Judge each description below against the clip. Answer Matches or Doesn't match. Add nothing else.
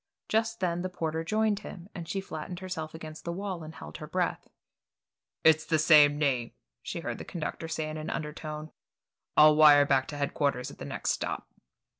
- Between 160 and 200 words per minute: Matches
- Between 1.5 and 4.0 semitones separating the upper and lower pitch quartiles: Matches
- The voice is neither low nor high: Matches